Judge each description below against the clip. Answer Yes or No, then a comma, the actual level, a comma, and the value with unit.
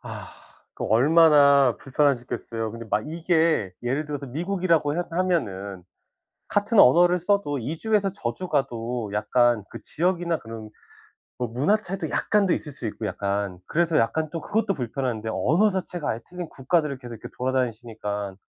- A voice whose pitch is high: No, medium, 140 Hz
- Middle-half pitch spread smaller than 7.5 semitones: Yes, wide, 7.0 semitones